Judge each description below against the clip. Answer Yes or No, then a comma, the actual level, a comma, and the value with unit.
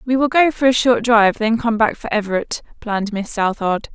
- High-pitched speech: Yes, high, 225 Hz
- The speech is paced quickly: Yes, fast, 230 wpm